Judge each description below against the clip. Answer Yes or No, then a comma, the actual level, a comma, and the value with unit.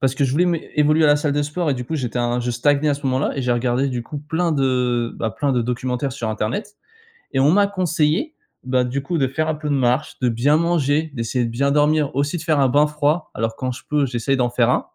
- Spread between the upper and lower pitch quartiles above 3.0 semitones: Yes, average, 3.4 semitones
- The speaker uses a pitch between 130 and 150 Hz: Yes, medium, 140 Hz